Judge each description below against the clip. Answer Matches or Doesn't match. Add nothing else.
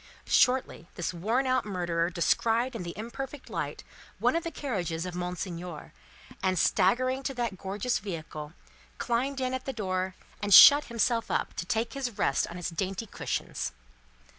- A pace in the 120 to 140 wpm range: Doesn't match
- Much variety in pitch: Matches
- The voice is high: Matches